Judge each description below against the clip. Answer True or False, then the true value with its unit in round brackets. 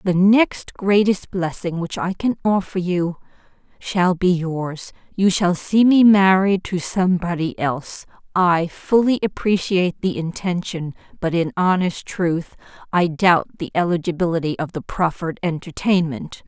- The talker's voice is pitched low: False (180 Hz)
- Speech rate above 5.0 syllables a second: False (4.4 syllables/s)